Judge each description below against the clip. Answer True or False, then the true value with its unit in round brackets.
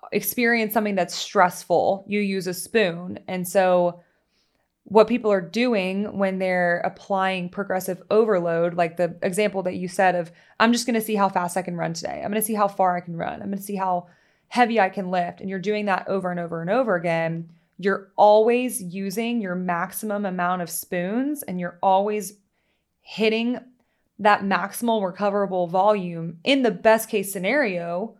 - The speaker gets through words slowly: False (185 wpm)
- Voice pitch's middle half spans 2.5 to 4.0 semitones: True (3.0 semitones)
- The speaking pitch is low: False (195 Hz)